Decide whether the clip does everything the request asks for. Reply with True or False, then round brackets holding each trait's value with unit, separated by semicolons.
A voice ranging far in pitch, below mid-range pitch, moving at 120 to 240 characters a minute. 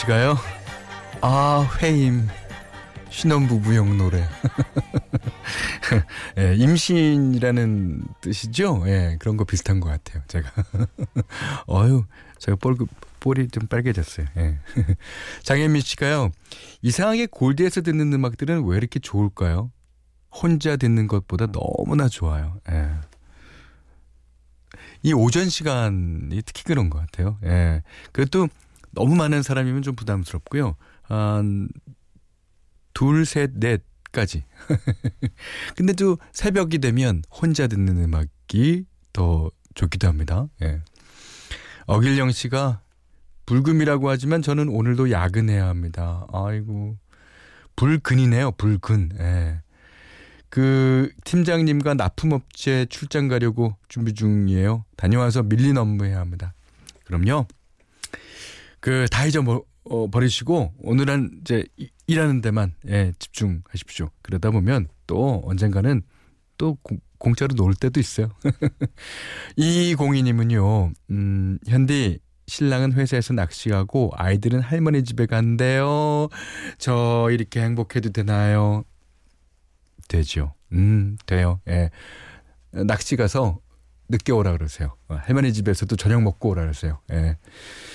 True (6.8 semitones; 110 Hz; 235 characters per minute)